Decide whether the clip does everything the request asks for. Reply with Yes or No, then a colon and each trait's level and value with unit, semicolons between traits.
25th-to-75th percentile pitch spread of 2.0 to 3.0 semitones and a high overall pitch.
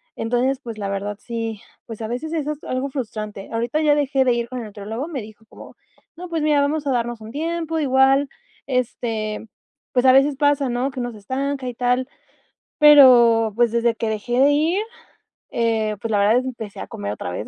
No: average, 3.8 semitones; high, 245 Hz